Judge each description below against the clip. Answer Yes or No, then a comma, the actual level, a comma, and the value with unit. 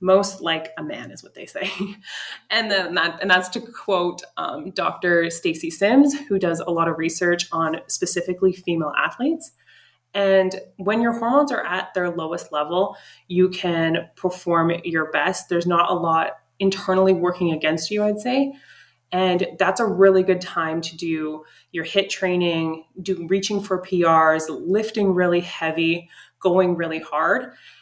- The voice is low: No, medium, 180 Hz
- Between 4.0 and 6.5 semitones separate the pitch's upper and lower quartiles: No, average, 2.7 semitones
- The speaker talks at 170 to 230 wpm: No, average, 160 wpm